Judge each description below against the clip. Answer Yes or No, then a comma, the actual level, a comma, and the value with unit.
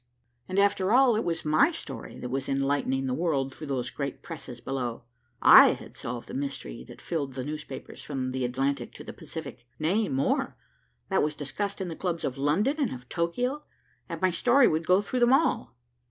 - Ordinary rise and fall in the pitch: No, wide, 6.3 semitones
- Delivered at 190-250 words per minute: Yes, average, 195 wpm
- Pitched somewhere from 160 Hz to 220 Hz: No, medium, 150 Hz